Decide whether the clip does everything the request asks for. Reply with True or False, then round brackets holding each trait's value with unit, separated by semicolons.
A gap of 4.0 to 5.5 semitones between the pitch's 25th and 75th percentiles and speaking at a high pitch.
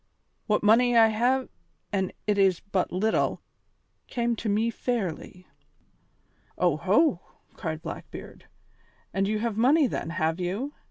True (4.4 semitones; 210 Hz)